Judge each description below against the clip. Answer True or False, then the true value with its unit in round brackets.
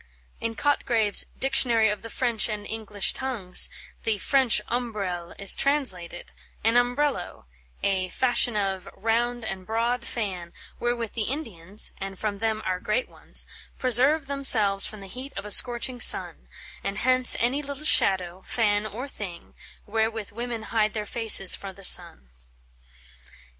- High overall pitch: True (220 Hz)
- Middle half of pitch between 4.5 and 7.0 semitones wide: False (3.6 semitones)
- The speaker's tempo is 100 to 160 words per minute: True (145 wpm)